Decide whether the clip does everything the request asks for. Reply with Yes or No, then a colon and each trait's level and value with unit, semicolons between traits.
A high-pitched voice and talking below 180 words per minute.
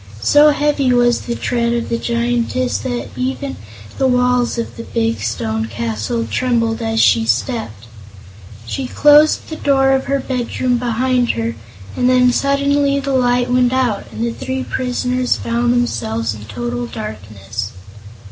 Yes: high, 245 Hz; average, 150 wpm